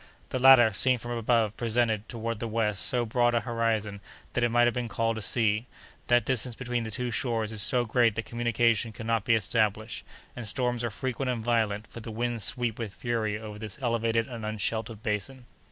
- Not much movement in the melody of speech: Yes, narrow, 1.7 semitones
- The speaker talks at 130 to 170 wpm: No, average, 200 wpm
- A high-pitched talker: No, low, 115 Hz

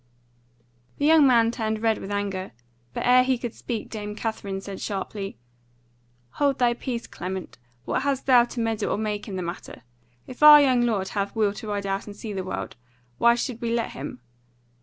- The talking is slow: No, average, 195 wpm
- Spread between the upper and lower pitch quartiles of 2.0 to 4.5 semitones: Yes, average, 3.5 semitones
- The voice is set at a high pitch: Yes, high, 220 Hz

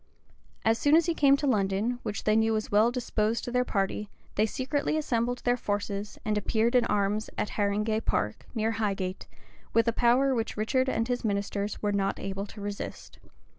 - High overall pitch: Yes, high, 220 Hz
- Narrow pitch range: No, average, 3.2 semitones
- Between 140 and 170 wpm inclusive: No, average, 190 wpm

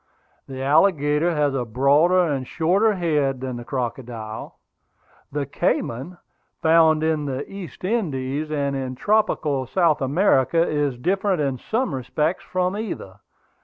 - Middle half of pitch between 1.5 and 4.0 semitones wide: No, average, 4.8 semitones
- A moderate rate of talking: No, slow, 130 wpm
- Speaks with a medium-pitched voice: Yes, medium, 150 Hz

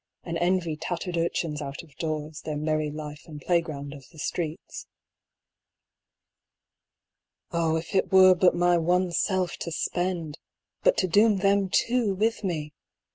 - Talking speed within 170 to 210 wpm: No, average, 145 wpm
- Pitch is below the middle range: No, medium, 170 Hz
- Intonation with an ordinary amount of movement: Yes, average, 3.3 semitones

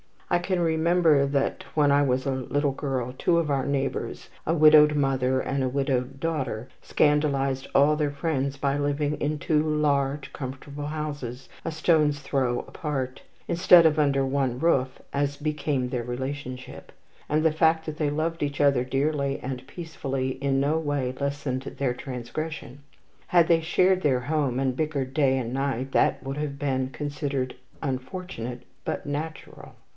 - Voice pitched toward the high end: No, medium, 140 Hz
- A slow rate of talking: No, average, 160 wpm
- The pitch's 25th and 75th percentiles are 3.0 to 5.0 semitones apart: No, narrow, 2.4 semitones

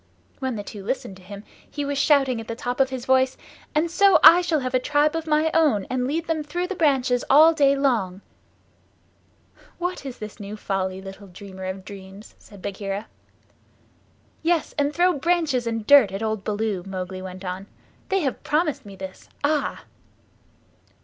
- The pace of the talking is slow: No, average, 180 wpm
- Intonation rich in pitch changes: Yes, wide, 7.2 semitones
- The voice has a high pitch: Yes, very high, 255 Hz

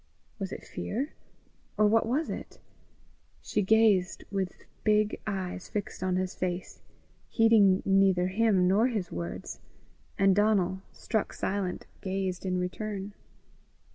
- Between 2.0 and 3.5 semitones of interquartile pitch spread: Yes, narrow, 2.5 semitones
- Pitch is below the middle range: No, high, 195 Hz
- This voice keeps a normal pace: No, slow, 125 wpm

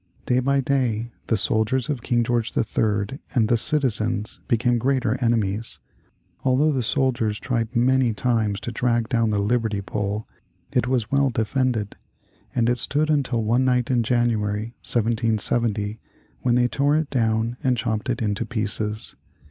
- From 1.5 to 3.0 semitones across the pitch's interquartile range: Yes, narrow, 2.6 semitones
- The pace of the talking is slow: No, average, 155 wpm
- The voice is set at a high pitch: No, low, 115 Hz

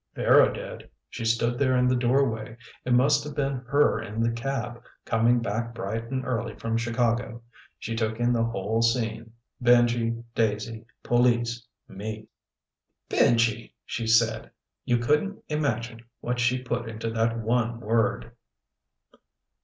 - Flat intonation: Yes, narrow, 1.4 semitones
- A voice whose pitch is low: Yes, low, 115 Hz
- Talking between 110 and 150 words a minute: Yes, average, 140 wpm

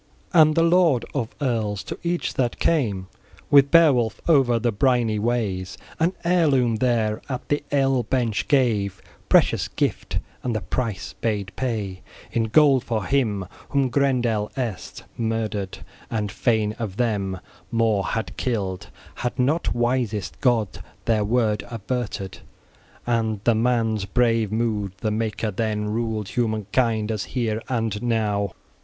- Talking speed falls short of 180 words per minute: Yes, average, 145 wpm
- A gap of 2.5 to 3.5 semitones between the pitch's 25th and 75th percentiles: Yes, average, 3.1 semitones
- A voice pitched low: Yes, low, 115 Hz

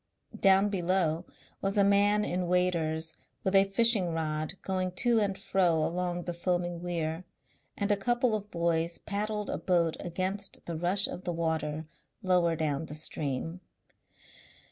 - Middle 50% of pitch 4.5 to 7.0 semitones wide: No, average, 3.1 semitones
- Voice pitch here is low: No, medium, 180 Hz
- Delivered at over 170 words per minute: No, average, 150 wpm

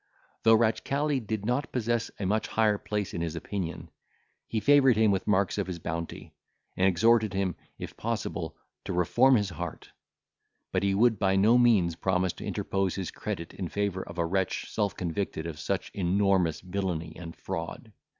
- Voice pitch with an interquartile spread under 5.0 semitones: Yes, average, 3.8 semitones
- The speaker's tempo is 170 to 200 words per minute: Yes, average, 175 wpm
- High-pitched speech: No, very low, 95 Hz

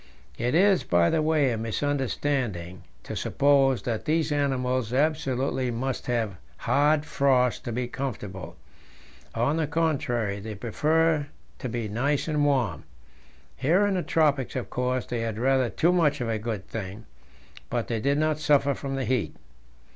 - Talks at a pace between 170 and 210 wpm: No, average, 160 wpm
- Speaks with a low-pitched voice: Yes, low, 130 Hz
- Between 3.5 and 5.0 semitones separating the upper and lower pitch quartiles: Yes, average, 4.2 semitones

